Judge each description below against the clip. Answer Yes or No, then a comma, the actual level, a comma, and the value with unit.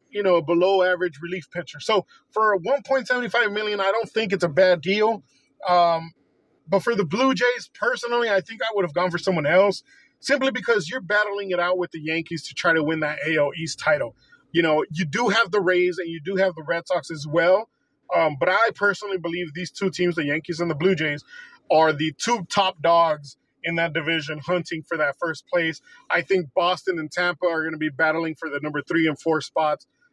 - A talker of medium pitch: Yes, medium, 180 Hz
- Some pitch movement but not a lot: Yes, average, 4.0 semitones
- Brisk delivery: Yes, fast, 220 wpm